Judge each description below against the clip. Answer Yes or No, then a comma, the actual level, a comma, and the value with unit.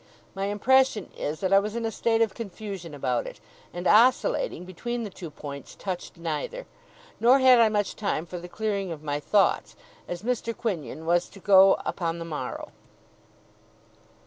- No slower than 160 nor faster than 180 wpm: Yes, average, 170 wpm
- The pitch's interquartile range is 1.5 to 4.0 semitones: No, average, 5.1 semitones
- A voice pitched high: Yes, high, 195 Hz